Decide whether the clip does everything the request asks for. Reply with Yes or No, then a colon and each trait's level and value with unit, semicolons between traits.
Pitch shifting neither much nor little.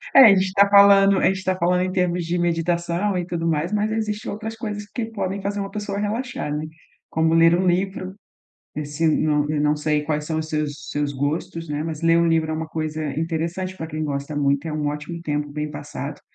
Yes: average, 4.0 semitones